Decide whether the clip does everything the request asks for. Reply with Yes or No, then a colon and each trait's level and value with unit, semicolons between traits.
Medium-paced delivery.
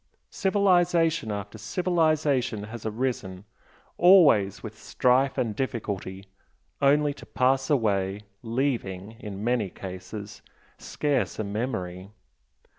No: slow, 100 wpm